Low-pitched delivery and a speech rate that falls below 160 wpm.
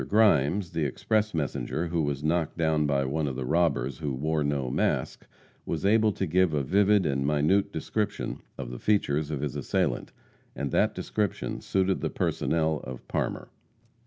No: very low, 80 Hz; average, 170 wpm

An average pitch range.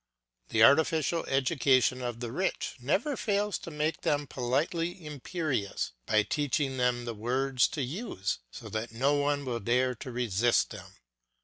Yes: average, 4.0 semitones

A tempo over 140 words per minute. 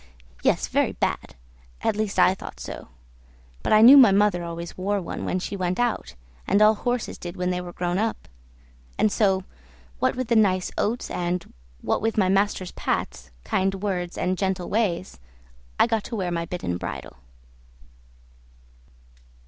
Yes: average, 170 wpm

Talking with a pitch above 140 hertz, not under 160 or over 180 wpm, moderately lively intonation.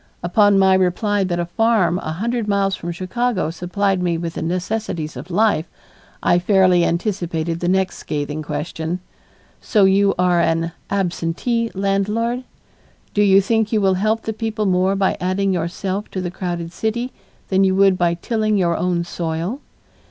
Yes: high, 190 Hz; average, 165 wpm; average, 3.1 semitones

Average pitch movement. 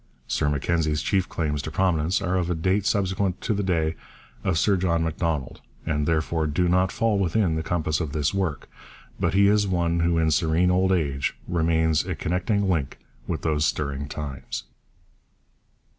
Yes: average, 3.1 semitones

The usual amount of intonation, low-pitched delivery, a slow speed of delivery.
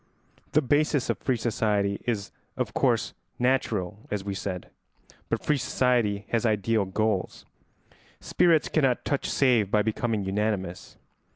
Yes: average, 4.0 semitones; low, 110 Hz; slow, 130 wpm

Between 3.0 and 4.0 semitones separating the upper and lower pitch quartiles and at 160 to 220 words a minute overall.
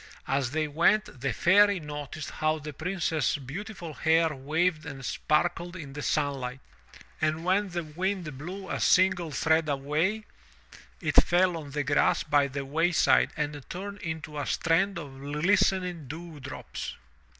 No: average, 3.5 semitones; average, 150 wpm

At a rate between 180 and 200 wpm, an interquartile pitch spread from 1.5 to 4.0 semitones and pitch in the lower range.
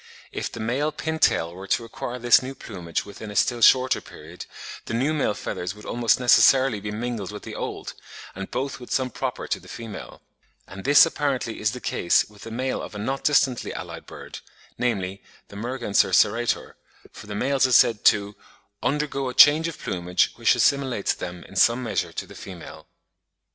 No: average, 190 wpm; average, 4.4 semitones; low, 115 Hz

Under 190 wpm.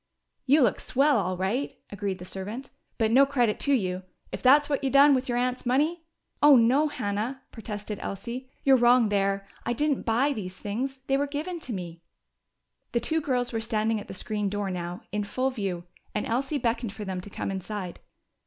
No: average, 200 wpm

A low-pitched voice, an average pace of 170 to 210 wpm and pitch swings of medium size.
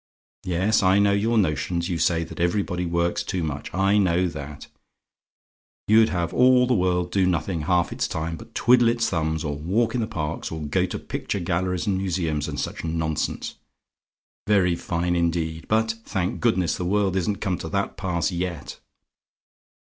Yes: very low, 90 Hz; average, 175 wpm; average, 3.3 semitones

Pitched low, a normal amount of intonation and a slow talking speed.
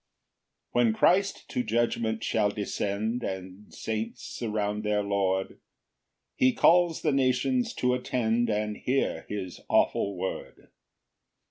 Yes: low, 110 Hz; average, 3.4 semitones; slow, 120 wpm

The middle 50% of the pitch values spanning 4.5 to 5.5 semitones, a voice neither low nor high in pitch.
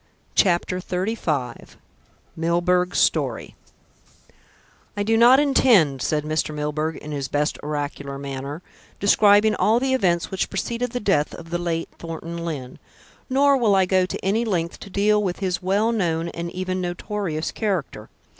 Yes: average, 4.8 semitones; medium, 180 Hz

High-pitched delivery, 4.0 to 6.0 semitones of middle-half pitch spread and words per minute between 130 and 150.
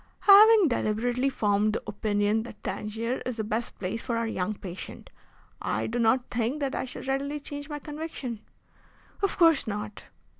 No: high, 235 Hz; average, 4.9 semitones; average, 165 wpm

